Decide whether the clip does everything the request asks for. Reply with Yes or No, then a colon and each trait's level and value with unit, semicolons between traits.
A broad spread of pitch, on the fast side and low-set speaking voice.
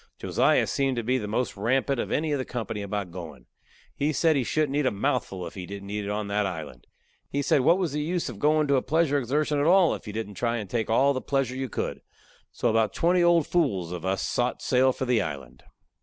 Yes: wide, 6.0 semitones; fast, 245 wpm; low, 125 Hz